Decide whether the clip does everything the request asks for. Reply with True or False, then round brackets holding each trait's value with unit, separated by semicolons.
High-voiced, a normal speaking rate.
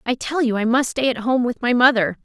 False (245 Hz; 295 wpm)